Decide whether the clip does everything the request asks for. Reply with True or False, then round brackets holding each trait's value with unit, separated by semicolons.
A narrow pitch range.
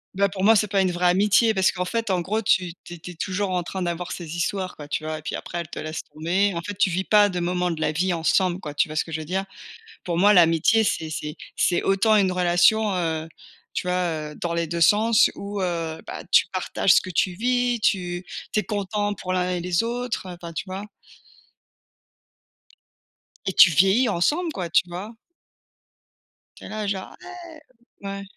False (3.0 semitones)